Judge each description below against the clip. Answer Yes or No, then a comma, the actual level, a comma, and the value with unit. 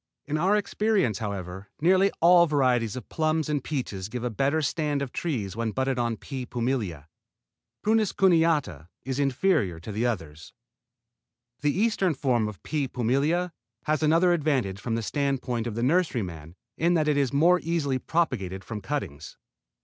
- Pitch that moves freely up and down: Yes, wide, 6.3 semitones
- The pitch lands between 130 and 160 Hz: Yes, low, 135 Hz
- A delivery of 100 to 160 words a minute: Yes, average, 155 wpm